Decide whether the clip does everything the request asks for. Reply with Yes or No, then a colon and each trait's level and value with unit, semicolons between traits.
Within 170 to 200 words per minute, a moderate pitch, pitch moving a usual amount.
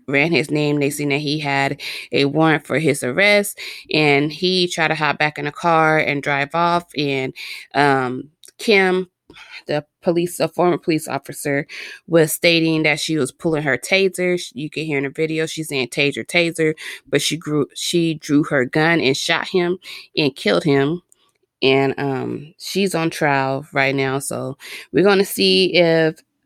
Yes: average, 175 wpm; medium, 155 Hz; average, 3.5 semitones